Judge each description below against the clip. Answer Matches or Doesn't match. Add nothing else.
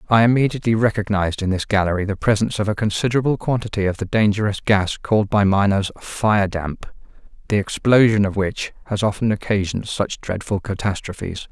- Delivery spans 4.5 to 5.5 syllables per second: Doesn't match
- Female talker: Doesn't match